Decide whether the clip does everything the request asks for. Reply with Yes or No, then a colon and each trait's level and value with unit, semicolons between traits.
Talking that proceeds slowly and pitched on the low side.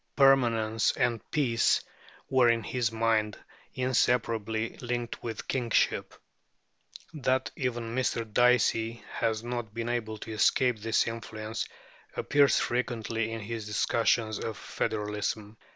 Yes: slow, 115 wpm; low, 115 Hz